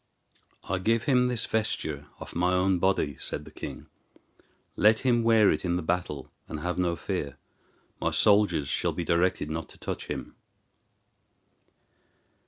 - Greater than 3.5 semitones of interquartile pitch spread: Yes, average, 5.1 semitones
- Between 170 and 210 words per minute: No, average, 155 wpm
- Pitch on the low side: Yes, very low, 90 Hz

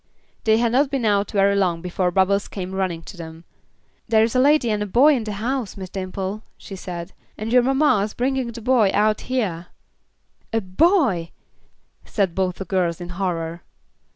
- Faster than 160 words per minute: Yes, average, 185 wpm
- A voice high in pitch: Yes, high, 200 Hz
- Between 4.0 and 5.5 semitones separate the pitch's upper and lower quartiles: Yes, average, 4.3 semitones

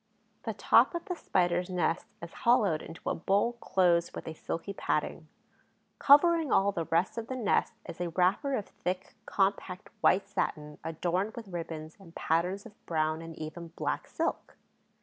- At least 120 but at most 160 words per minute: No, average, 170 wpm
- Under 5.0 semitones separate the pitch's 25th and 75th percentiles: Yes, average, 3.6 semitones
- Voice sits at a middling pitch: Yes, medium, 180 Hz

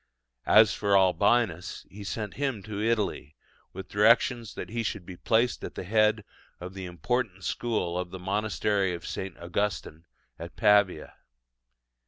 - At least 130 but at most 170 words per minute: Yes, average, 150 wpm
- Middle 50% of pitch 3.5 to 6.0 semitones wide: No, average, 3.1 semitones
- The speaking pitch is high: No, low, 100 Hz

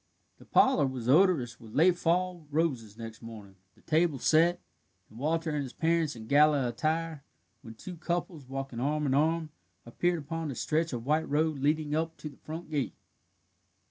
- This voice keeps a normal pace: Yes, average, 175 wpm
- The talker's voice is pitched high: No, medium, 150 Hz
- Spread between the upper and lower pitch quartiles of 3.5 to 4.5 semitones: Yes, average, 3.9 semitones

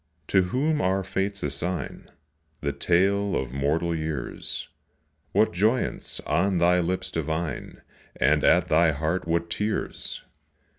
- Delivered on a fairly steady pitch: No, average, 3.6 semitones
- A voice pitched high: No, very low, 85 Hz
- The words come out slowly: Yes, slow, 120 wpm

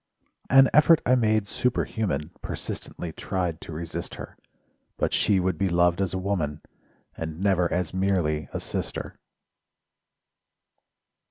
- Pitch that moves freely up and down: No, average, 3.1 semitones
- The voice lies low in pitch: Yes, very low, 90 Hz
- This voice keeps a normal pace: No, slow, 125 wpm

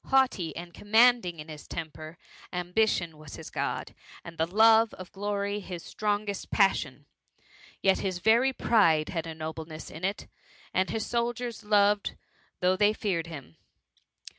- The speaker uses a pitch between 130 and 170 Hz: No, high, 190 Hz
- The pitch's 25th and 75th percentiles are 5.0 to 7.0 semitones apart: No, average, 4.6 semitones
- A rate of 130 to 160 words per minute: Yes, average, 155 wpm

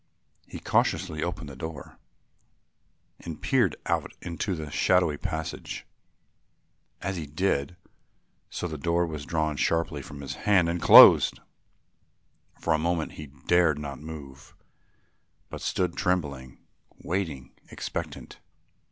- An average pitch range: Yes, average, 3.1 semitones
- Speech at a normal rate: No, slow, 120 wpm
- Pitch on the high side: No, very low, 80 Hz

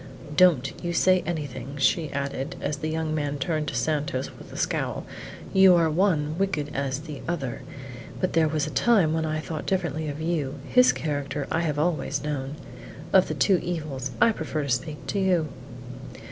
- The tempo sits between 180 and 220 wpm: Yes, average, 190 wpm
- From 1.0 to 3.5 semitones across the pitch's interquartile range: Yes, average, 3.1 semitones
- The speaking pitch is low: No, medium, 155 Hz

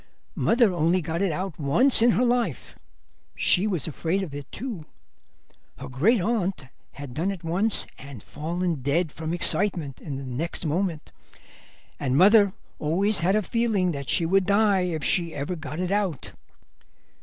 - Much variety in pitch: No, average, 4.7 semitones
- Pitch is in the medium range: Yes, medium, 175 Hz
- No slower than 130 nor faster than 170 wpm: Yes, average, 160 wpm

